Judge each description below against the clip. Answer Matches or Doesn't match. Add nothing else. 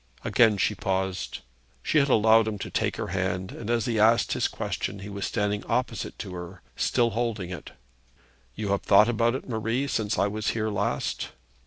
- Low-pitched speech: Matches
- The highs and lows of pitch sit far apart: Doesn't match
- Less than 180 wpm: Doesn't match